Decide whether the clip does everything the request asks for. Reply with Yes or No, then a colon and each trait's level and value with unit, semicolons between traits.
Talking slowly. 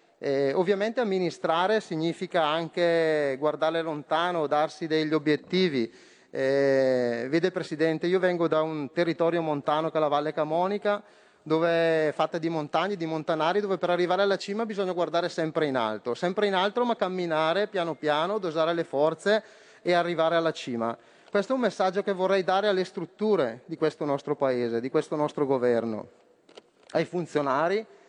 No: average, 155 wpm